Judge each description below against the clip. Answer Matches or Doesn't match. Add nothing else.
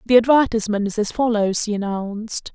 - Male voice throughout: Doesn't match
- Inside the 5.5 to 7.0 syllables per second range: Matches